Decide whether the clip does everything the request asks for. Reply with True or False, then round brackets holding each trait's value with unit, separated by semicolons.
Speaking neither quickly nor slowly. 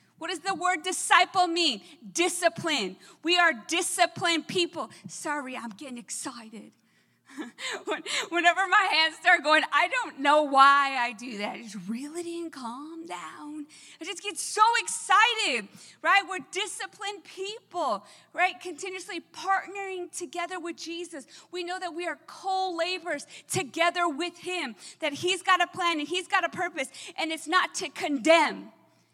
True (150 wpm)